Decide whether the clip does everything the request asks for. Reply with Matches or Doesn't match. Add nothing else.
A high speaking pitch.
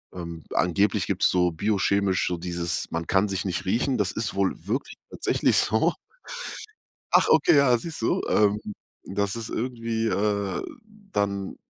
Doesn't match